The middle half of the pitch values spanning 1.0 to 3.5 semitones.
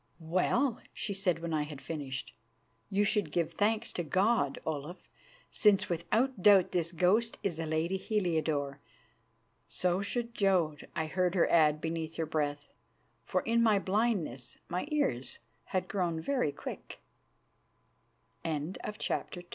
No: average, 4.5 semitones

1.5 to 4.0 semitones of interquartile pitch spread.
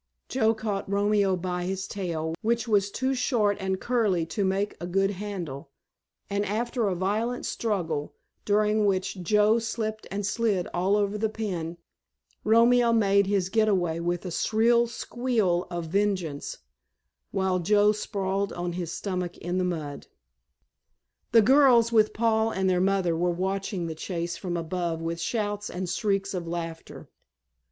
Yes: average, 3.4 semitones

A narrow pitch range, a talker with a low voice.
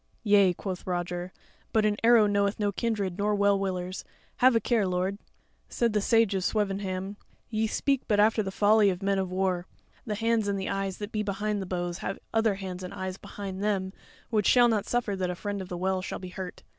No: narrow, 2.2 semitones; high, 200 Hz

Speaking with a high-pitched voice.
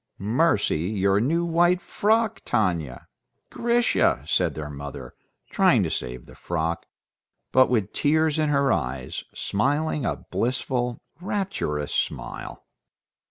No: low, 125 Hz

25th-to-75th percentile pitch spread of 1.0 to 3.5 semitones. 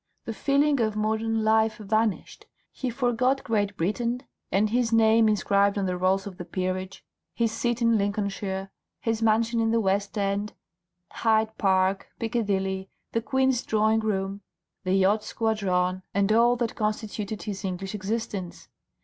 Yes: narrow, 2.6 semitones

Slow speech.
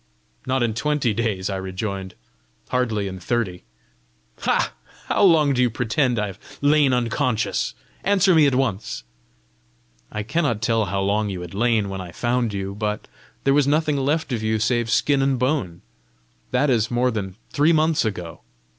No: average, 170 wpm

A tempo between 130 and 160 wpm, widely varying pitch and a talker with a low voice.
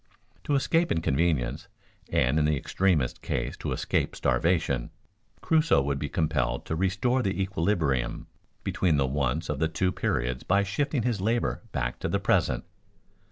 Yes: average, 155 wpm; wide, 6.2 semitones; very low, 80 Hz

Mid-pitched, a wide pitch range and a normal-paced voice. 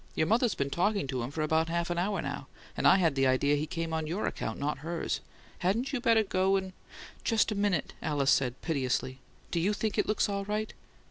No: medium, 170 Hz; wide, 5.8 semitones; fast, 225 wpm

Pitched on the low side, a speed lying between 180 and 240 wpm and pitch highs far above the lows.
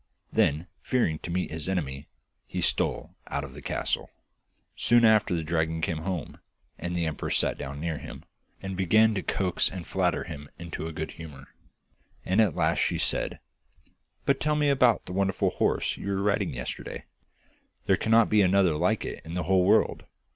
No: very low, 90 Hz; average, 185 wpm; average, 3.8 semitones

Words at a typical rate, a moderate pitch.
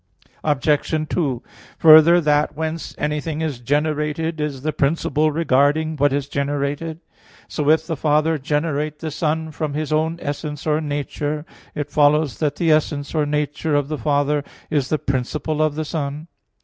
Yes: average, 160 wpm; medium, 150 Hz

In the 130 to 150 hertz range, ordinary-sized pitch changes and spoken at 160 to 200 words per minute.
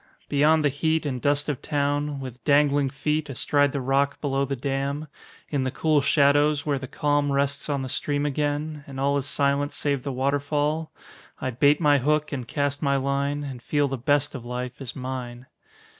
No: medium, 140 Hz; narrow, 1.3 semitones; average, 190 wpm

